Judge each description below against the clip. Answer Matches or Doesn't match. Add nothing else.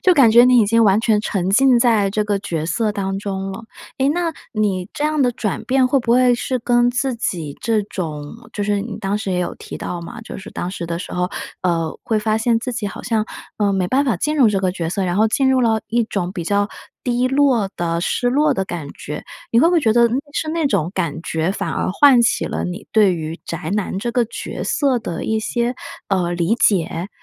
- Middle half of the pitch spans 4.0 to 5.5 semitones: Matches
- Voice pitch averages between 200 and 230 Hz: Matches